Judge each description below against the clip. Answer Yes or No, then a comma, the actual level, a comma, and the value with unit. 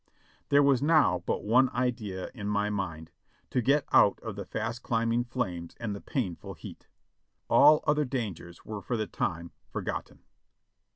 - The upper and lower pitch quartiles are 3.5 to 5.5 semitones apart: Yes, average, 4.7 semitones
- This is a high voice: No, low, 115 Hz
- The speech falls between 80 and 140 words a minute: No, average, 165 wpm